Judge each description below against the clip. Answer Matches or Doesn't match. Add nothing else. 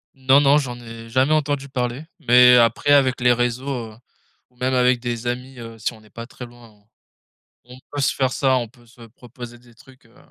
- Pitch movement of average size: Doesn't match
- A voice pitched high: Doesn't match